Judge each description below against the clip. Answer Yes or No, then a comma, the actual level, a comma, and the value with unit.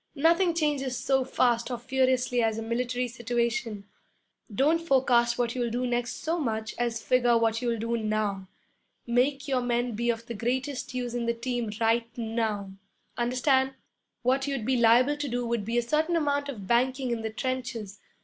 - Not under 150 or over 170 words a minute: No, average, 180 wpm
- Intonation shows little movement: Yes, narrow, 2.2 semitones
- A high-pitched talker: Yes, high, 240 Hz